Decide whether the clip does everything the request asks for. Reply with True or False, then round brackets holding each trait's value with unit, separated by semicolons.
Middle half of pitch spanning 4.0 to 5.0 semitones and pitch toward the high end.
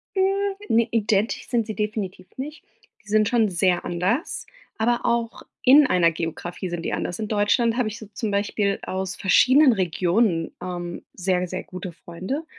True (4.5 semitones; 205 Hz)